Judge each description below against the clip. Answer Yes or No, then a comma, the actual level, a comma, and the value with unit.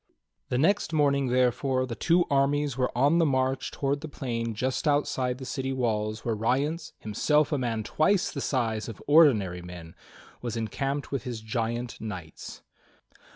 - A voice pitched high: No, low, 130 Hz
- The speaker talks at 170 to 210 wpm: No, average, 160 wpm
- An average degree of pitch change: Yes, average, 4.1 semitones